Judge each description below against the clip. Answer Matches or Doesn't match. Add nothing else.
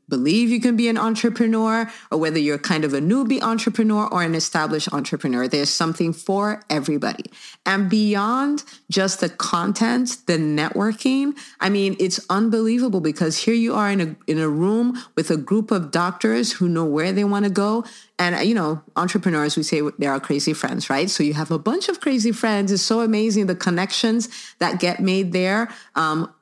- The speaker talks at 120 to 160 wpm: Doesn't match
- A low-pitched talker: Doesn't match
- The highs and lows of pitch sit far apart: Matches